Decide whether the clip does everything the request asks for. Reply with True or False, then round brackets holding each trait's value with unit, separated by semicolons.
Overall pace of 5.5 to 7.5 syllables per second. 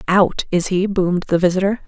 True (5.6 syllables/s)